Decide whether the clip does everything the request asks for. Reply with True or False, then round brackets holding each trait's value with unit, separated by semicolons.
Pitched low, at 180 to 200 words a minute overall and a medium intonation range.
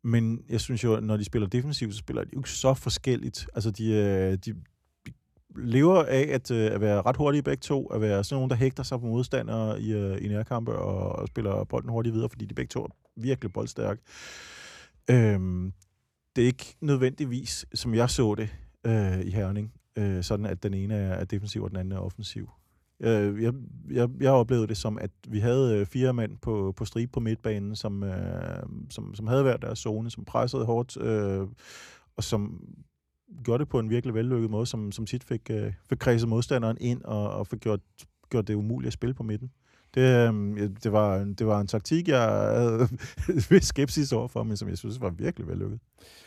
True (115 Hz; 195 wpm; 3.0 semitones)